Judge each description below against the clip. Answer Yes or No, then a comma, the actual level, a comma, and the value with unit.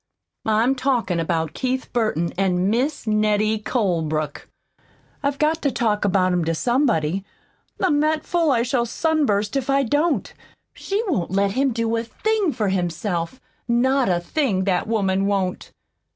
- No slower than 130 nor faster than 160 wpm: Yes, average, 150 wpm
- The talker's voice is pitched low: No, high, 220 Hz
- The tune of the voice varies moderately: No, wide, 6.4 semitones